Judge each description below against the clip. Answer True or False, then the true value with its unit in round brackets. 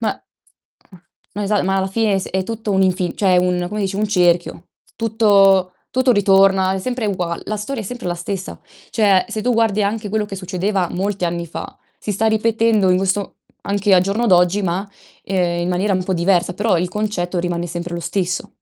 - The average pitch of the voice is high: True (195 Hz)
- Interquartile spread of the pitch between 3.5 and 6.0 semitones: False (2.6 semitones)